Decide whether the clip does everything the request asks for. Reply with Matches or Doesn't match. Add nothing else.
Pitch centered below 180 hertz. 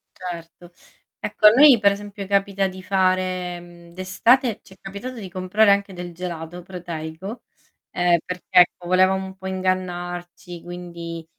Doesn't match